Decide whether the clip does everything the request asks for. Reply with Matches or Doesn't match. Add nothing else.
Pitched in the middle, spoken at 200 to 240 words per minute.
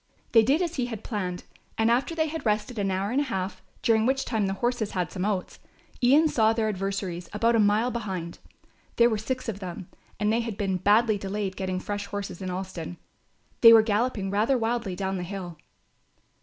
Doesn't match